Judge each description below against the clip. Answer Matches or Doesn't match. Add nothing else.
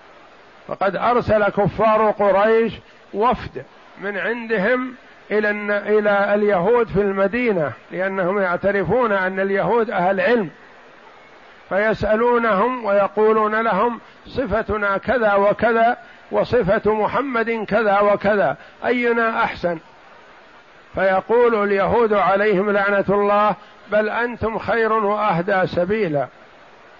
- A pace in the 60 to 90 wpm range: Matches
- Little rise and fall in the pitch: Matches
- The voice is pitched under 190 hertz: Doesn't match